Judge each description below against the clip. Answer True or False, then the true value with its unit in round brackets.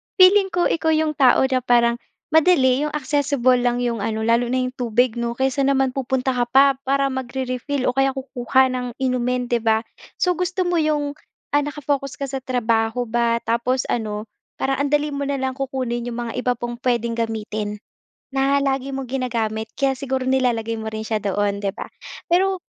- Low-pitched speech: False (255 Hz)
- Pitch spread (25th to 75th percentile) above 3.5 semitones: False (2.7 semitones)